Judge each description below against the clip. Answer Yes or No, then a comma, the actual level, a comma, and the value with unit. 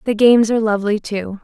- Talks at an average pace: No, fast, 210 wpm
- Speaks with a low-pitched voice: No, high, 215 Hz